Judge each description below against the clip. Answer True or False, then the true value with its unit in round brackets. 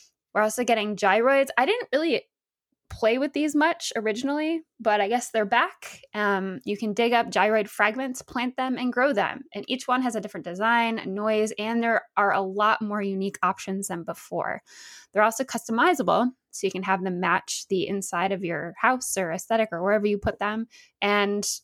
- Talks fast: False (190 wpm)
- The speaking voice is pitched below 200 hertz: False (220 Hz)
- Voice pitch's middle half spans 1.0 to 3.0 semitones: False (3.8 semitones)